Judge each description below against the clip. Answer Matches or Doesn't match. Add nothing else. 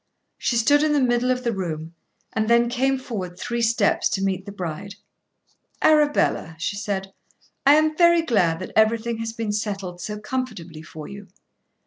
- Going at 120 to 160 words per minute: Doesn't match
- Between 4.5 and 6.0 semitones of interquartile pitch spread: Matches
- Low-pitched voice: Doesn't match